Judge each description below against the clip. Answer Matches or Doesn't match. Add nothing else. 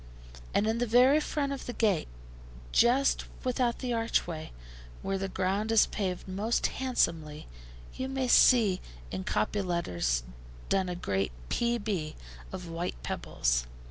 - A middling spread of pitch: Doesn't match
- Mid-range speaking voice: Doesn't match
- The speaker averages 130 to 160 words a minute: Matches